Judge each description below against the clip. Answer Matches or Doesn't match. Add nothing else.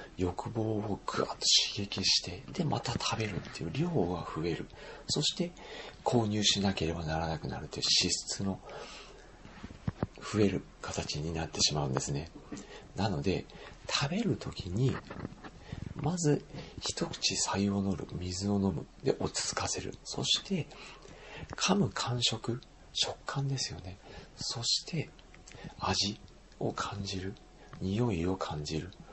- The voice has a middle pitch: Doesn't match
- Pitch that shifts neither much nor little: Matches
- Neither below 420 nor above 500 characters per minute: Doesn't match